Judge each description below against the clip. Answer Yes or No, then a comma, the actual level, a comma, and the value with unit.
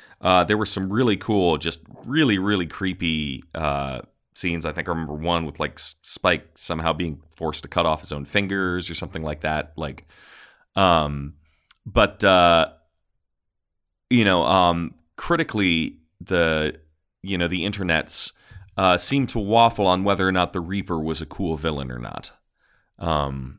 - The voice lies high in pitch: No, very low, 85 Hz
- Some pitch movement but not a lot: Yes, average, 3.4 semitones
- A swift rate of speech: No, average, 160 wpm